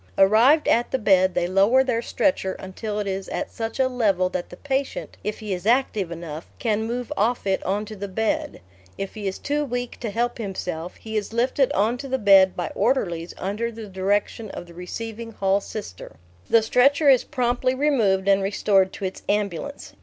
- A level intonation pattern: No, average, 4.3 semitones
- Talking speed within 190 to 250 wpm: Yes, average, 200 wpm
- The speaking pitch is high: Yes, high, 215 Hz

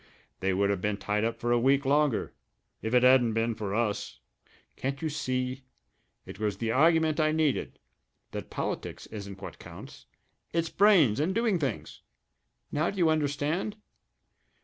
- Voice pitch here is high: No, low, 130 Hz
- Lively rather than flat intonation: Yes, wide, 6.1 semitones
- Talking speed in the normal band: Yes, average, 160 wpm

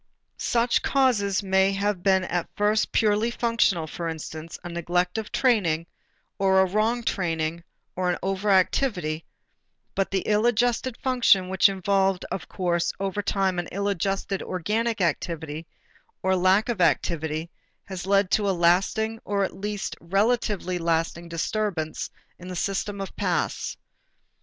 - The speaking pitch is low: No, high, 190 Hz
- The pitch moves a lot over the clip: No, average, 3.2 semitones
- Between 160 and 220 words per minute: No, average, 145 wpm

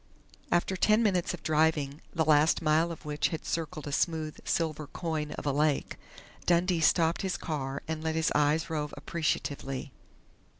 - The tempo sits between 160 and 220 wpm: Yes, average, 165 wpm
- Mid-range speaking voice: Yes, medium, 160 Hz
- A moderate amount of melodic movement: No, narrow, 2.1 semitones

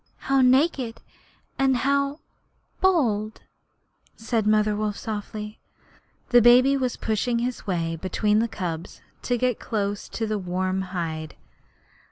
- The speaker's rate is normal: No, slow, 125 wpm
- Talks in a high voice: Yes, high, 220 Hz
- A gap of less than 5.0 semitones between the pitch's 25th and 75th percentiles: Yes, average, 4.0 semitones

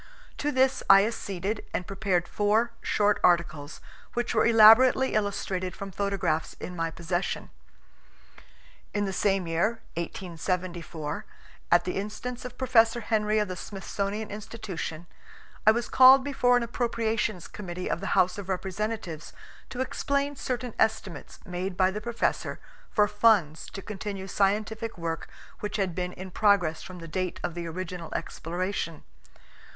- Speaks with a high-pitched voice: Yes, high, 200 Hz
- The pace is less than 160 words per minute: Yes, average, 145 wpm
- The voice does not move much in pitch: No, average, 3.7 semitones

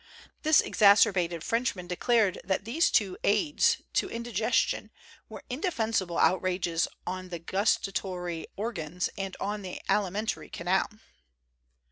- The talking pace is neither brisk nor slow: No, slow, 120 wpm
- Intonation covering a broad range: No, average, 3.8 semitones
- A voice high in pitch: Yes, high, 195 Hz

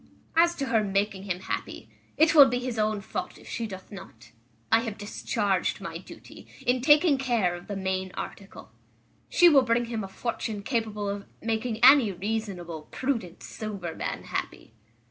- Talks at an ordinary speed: Yes, average, 170 wpm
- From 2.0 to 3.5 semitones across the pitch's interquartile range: No, average, 4.2 semitones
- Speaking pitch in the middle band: No, high, 215 Hz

